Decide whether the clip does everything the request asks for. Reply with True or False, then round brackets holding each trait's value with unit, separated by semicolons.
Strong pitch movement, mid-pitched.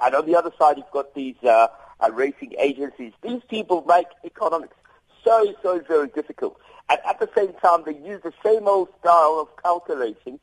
True (6.8 semitones; 175 Hz)